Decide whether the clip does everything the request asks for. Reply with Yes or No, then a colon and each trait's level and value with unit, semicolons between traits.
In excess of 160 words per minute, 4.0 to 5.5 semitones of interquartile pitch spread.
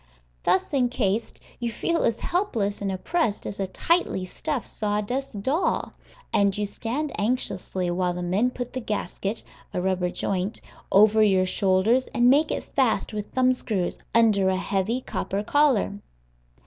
No: average, 150 wpm; average, 4.7 semitones